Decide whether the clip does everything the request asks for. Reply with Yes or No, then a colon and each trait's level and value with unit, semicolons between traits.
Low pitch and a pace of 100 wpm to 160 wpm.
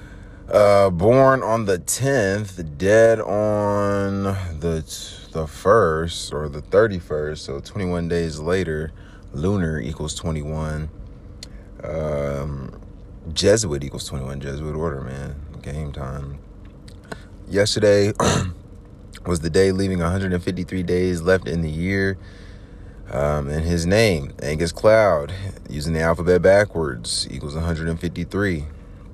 Yes: very low, 90 Hz; slow, 135 wpm